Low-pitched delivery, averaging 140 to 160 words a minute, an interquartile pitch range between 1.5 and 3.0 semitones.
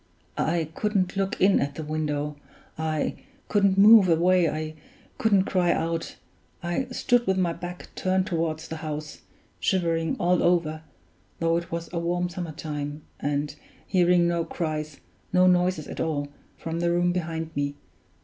No: medium, 170 Hz; average, 155 wpm; narrow, 2.6 semitones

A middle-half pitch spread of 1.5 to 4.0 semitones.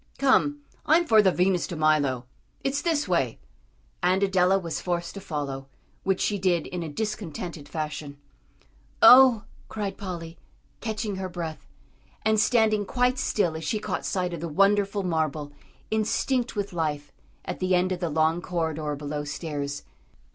No: average, 4.9 semitones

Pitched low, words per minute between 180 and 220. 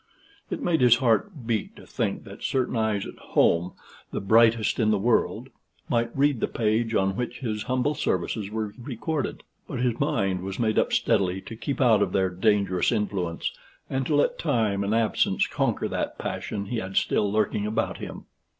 Yes: low, 110 Hz; average, 185 wpm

